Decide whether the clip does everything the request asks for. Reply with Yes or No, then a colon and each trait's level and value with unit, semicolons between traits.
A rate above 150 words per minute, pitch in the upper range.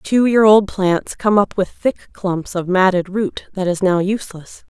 Yes: average, 200 wpm; high, 195 Hz